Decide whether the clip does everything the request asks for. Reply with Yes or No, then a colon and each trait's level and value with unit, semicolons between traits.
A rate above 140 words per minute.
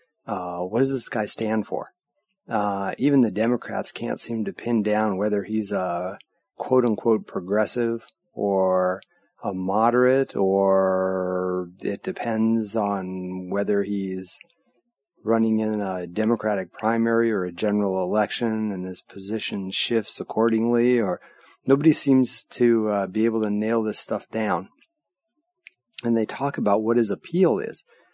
No: slow, 135 wpm